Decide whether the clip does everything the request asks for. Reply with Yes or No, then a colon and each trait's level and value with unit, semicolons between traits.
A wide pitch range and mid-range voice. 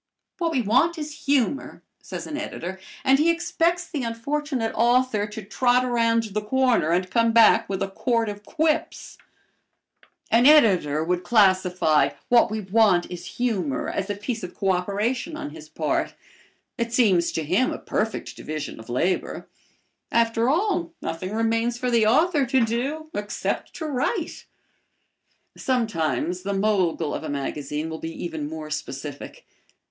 No: wide, 6.2 semitones; high, 225 Hz